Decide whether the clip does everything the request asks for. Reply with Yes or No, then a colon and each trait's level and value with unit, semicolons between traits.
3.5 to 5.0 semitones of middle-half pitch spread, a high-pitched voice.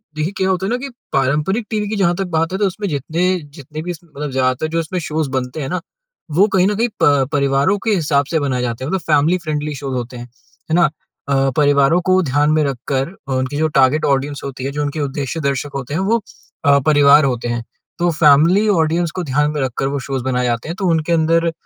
No: average, 3.9 semitones; medium, 150 Hz